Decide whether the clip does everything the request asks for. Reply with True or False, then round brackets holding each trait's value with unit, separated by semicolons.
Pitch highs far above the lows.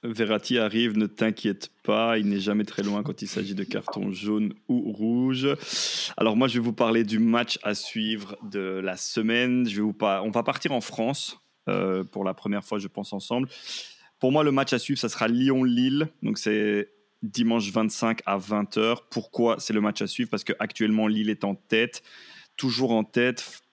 False (3.0 semitones)